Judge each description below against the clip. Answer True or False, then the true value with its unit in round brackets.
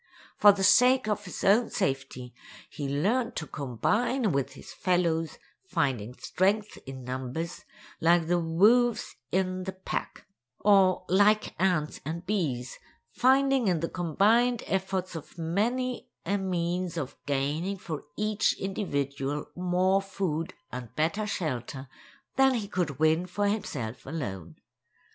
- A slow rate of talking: True (130 wpm)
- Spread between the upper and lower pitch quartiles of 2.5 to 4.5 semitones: False (5.5 semitones)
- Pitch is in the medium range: True (180 Hz)